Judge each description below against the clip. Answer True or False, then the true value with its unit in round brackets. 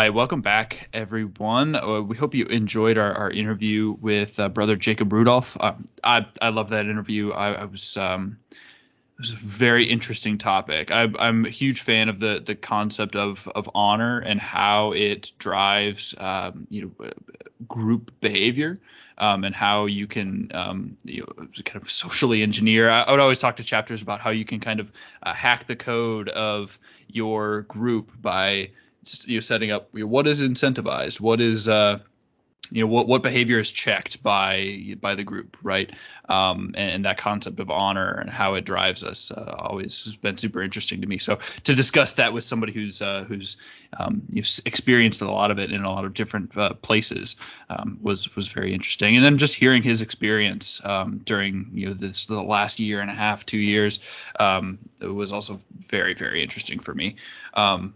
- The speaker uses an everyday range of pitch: False (2.1 semitones)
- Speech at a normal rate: True (195 wpm)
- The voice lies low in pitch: True (105 Hz)